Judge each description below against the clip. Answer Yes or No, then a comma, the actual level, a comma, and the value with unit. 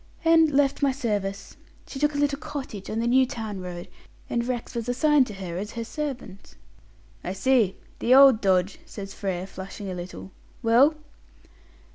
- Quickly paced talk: No, average, 170 wpm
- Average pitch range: No, wide, 5.7 semitones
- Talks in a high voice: Yes, high, 230 Hz